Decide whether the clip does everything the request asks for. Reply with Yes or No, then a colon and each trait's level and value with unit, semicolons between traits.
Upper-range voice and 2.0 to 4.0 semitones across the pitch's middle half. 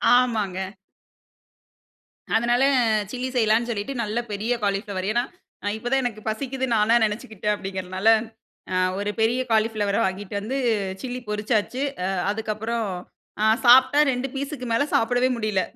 Yes: high, 220 Hz; average, 2.9 semitones